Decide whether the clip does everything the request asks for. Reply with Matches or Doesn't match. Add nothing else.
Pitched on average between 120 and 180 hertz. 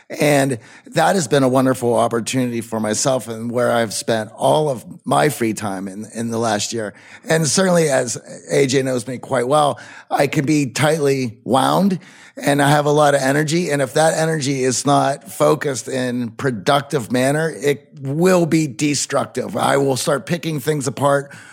Matches